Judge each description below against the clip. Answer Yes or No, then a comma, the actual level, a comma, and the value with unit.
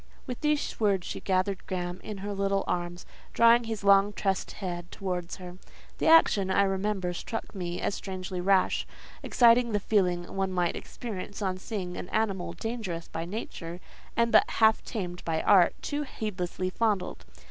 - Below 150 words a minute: No, average, 165 wpm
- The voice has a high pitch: Yes, high, 195 Hz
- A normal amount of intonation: Yes, average, 3.3 semitones